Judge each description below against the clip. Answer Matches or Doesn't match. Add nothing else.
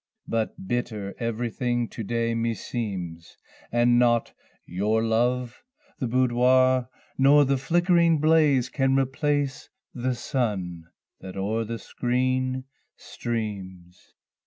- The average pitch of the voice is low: Matches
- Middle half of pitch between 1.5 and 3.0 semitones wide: Matches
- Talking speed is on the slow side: Matches